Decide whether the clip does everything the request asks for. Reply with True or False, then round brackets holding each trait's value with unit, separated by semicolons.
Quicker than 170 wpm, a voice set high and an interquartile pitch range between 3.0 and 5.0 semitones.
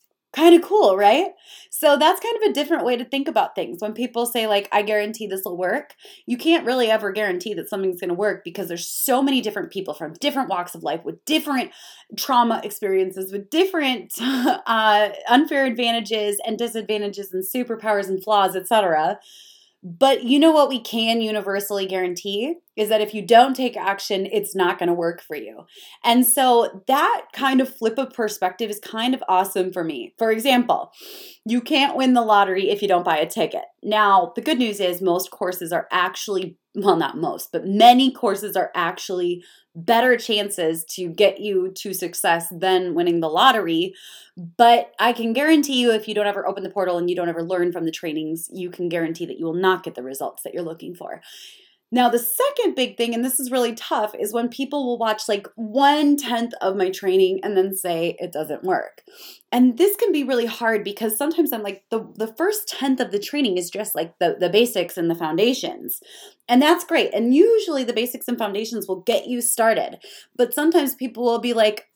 False (205 wpm; 220 Hz; 5.6 semitones)